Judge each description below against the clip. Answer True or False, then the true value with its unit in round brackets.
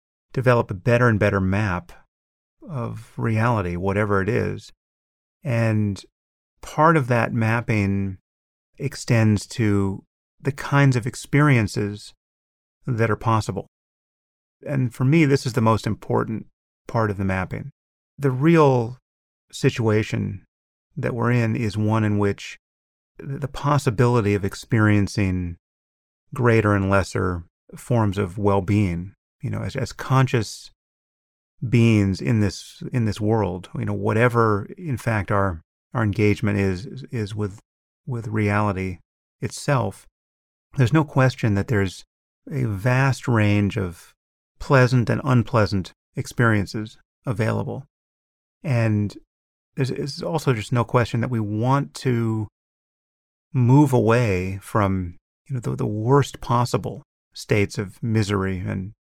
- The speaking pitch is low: True (110 Hz)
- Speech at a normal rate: False (125 wpm)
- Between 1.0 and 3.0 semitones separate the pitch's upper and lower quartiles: False (4.1 semitones)